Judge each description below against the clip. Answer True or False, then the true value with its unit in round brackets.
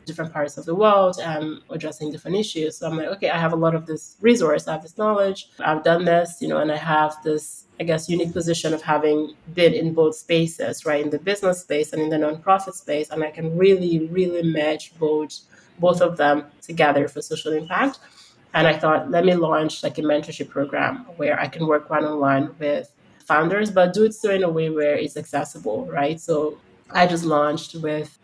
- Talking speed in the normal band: False (215 wpm)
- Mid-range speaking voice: True (160 Hz)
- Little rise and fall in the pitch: True (2.2 semitones)